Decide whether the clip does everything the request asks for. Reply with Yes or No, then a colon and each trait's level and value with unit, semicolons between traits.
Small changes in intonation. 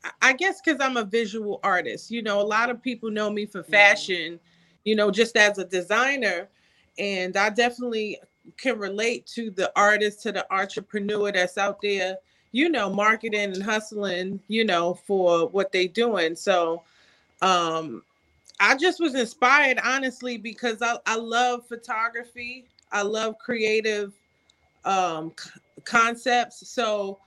No: average, 3.3 semitones